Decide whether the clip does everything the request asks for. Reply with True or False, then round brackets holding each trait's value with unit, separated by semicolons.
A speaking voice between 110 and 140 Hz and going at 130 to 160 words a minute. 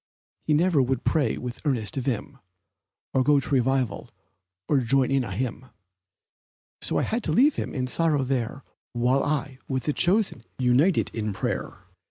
False (135 Hz; 170 wpm)